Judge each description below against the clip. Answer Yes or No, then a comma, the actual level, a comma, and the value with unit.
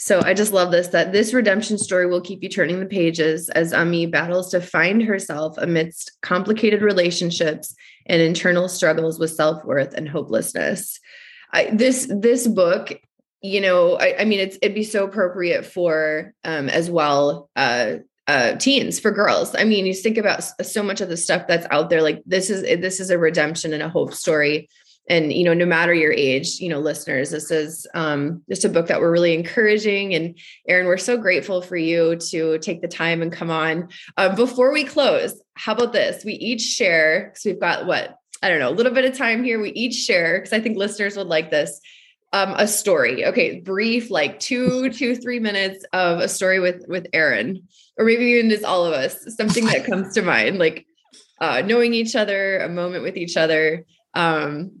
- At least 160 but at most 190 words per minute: No, average, 200 wpm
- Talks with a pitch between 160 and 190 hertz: Yes, medium, 185 Hz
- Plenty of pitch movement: No, average, 4.5 semitones